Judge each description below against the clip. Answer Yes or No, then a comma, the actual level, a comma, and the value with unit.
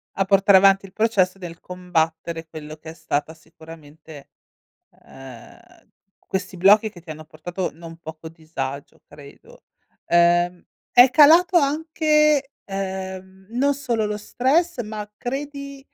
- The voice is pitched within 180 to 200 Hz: Yes, high, 190 Hz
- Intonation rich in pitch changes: Yes, wide, 7.0 semitones